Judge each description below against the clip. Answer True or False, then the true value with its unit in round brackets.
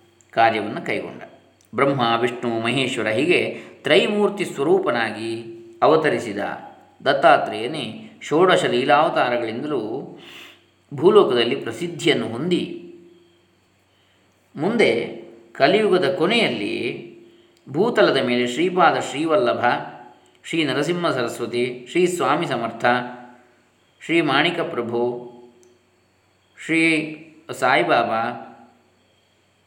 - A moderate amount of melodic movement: False (6.0 semitones)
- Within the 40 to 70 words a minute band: True (65 wpm)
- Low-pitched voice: True (120 Hz)